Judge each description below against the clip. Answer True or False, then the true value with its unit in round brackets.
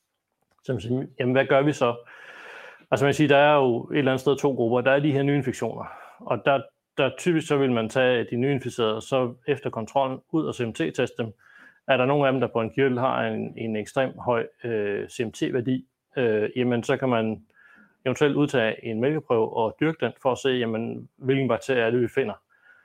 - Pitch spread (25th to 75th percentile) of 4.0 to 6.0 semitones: False (2.8 semitones)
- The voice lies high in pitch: False (130 Hz)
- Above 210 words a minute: False (205 wpm)